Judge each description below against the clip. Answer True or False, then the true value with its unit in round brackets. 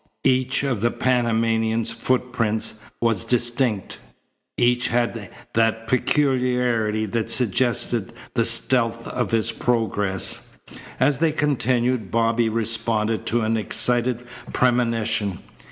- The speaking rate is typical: False (105 wpm)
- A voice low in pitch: True (115 Hz)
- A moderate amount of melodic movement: False (1.9 semitones)